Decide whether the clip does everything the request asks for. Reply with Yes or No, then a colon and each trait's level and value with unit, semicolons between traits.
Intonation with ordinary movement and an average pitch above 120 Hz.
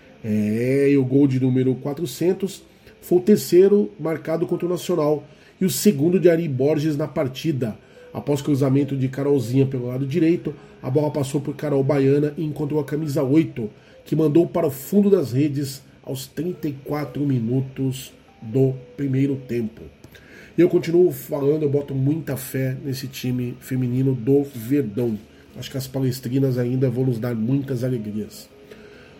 Yes: average, 3.1 semitones; medium, 140 Hz